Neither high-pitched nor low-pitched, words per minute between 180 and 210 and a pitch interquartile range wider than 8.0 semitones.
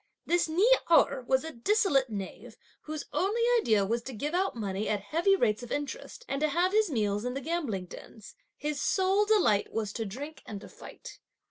No: very high, 280 Hz; average, 200 wpm; wide, 8.5 semitones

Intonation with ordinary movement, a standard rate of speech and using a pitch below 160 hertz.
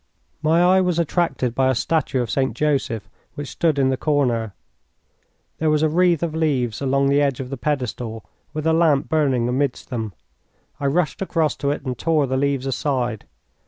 Yes: average, 3.5 semitones; average, 190 wpm; medium, 140 Hz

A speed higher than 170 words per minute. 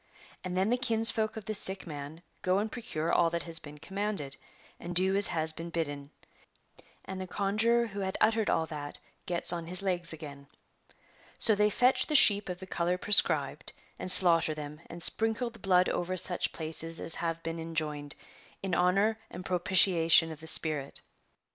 Yes: average, 180 wpm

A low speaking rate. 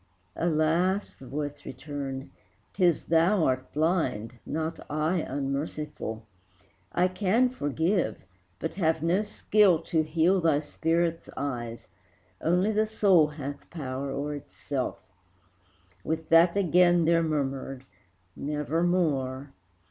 Yes: slow, 110 wpm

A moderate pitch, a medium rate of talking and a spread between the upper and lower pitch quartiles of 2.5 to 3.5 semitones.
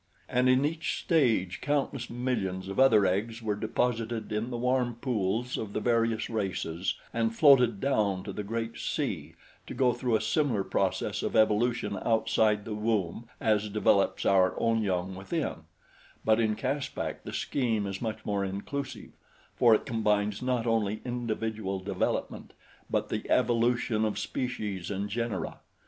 No: low, 110 Hz; average, 155 wpm; average, 3.0 semitones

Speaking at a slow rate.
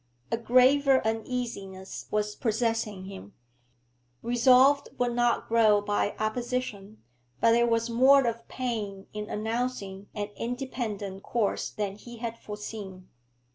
Yes: slow, 120 wpm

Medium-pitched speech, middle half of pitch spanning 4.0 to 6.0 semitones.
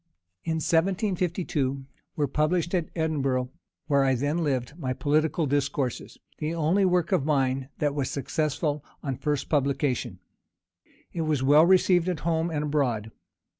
No: medium, 150 Hz; average, 3.3 semitones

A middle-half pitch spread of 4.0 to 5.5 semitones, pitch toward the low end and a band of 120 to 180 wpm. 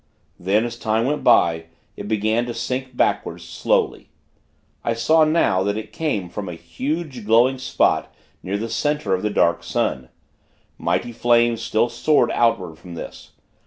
Yes: average, 4.4 semitones; low, 115 Hz; average, 160 wpm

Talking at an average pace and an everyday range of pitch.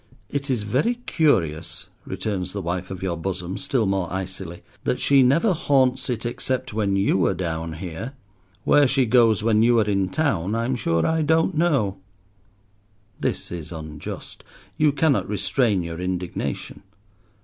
No: average, 155 wpm; wide, 6.6 semitones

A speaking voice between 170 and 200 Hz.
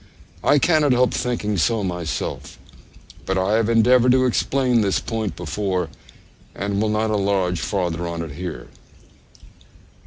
No: low, 105 Hz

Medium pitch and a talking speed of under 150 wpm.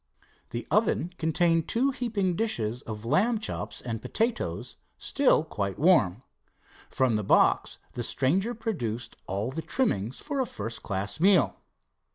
Yes: medium, 160 Hz; average, 140 wpm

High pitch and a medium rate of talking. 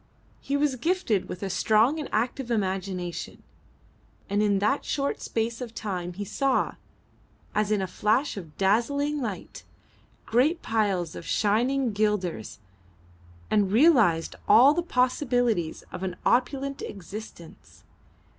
No: high, 220 Hz; slow, 125 wpm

